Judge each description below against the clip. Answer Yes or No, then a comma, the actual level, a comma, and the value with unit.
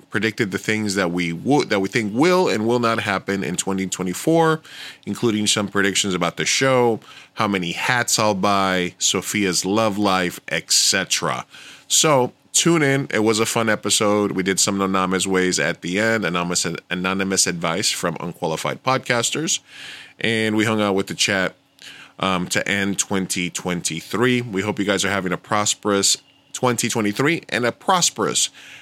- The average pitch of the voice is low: Yes, low, 100 Hz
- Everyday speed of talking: Yes, average, 160 wpm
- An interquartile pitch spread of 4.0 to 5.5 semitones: No, average, 3.2 semitones